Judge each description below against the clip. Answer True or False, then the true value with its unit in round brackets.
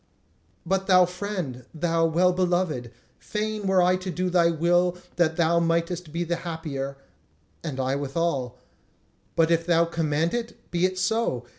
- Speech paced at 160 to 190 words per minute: False (150 wpm)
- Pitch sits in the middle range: True (170 Hz)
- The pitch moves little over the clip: True (2.3 semitones)